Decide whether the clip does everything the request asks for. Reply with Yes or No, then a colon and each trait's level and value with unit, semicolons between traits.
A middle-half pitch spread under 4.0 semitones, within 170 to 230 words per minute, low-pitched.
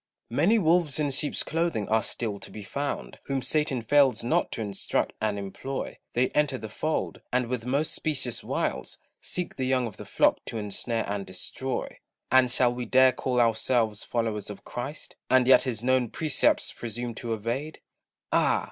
Yes: average, 3.5 semitones; average, 175 wpm; low, 125 Hz